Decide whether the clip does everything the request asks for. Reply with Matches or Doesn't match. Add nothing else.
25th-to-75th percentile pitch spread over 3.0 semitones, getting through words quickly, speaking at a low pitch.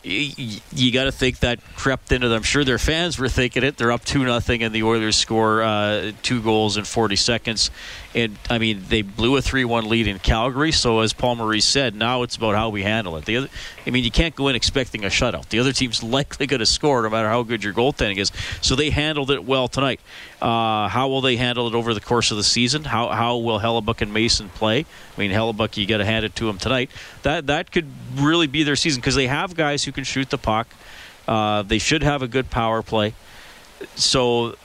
Matches